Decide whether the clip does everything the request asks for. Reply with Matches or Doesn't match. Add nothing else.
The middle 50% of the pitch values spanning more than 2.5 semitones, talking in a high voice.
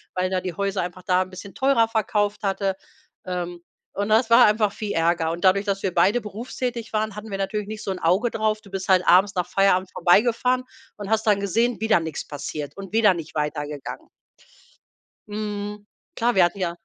Matches